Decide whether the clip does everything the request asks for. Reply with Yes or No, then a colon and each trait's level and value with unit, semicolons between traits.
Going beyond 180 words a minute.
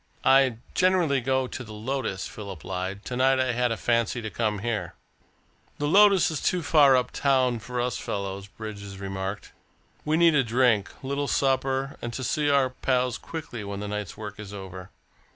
Yes: average, 190 wpm